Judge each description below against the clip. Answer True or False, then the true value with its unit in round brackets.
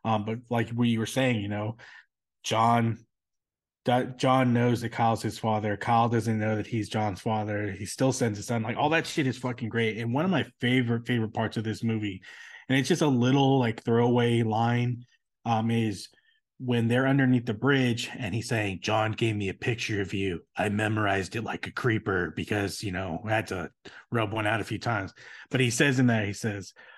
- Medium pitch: False (115 Hz)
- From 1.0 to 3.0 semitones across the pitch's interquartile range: True (2.5 semitones)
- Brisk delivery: True (215 wpm)